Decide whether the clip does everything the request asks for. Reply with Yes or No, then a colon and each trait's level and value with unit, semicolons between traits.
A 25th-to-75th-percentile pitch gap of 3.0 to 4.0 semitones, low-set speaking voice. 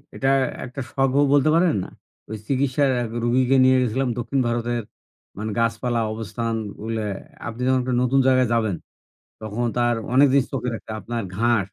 No: narrow, 2.5 semitones; low, 120 Hz